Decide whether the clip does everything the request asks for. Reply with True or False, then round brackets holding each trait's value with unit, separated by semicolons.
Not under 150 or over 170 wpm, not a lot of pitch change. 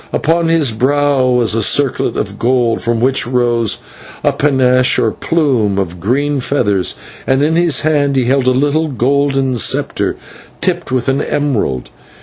False (155 wpm; 3.3 semitones)